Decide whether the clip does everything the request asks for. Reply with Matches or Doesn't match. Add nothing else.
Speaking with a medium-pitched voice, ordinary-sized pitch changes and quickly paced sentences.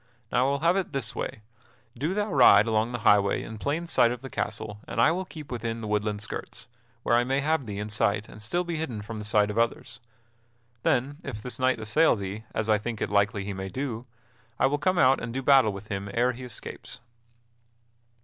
Doesn't match